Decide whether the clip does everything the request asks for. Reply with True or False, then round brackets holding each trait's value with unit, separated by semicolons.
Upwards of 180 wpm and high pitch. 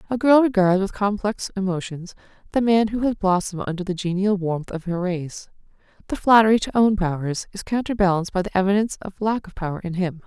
True (200 wpm; 195 Hz)